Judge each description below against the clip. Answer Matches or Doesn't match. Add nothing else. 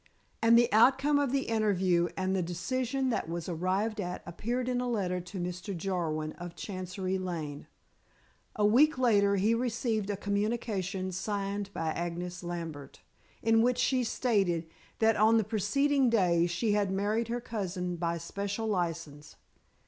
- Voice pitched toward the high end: Matches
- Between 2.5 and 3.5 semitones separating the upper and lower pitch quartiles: Doesn't match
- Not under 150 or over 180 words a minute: Matches